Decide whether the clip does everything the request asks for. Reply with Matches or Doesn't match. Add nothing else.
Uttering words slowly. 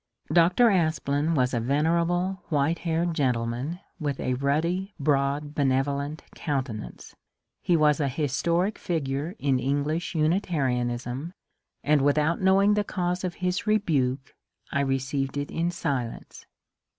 Matches